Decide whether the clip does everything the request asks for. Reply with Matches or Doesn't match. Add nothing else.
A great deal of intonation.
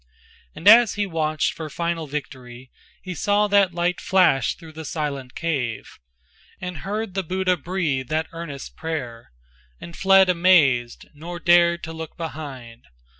Doesn't match